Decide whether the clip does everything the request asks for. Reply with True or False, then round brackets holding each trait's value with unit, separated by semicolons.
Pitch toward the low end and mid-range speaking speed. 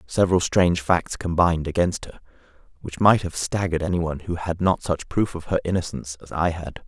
True (85 Hz; 190 wpm)